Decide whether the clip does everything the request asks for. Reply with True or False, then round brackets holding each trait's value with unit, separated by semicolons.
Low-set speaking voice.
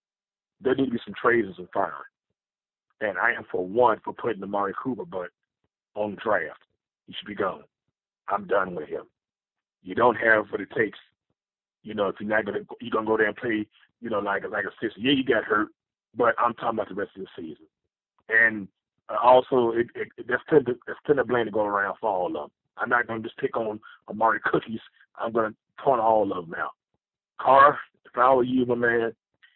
True (115 Hz)